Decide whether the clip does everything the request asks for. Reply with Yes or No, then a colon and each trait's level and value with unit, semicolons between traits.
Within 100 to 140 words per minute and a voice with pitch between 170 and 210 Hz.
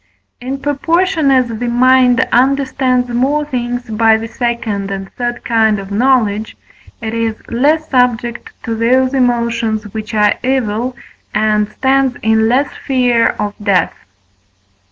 No: slow, 135 wpm; high, 240 Hz